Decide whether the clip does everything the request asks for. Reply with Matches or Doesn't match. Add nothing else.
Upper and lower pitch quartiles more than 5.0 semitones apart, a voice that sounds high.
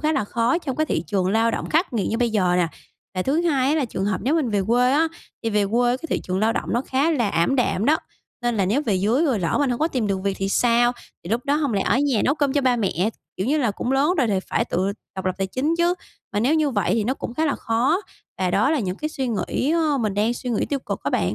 Matches